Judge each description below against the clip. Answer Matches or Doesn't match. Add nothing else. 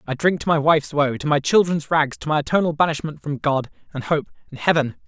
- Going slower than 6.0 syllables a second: Doesn't match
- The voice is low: Doesn't match